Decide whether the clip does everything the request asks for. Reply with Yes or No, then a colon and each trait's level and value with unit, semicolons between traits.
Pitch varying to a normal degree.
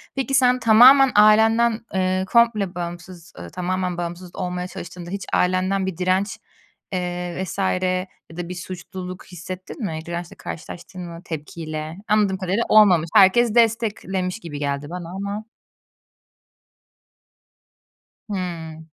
Yes: average, 3.3 semitones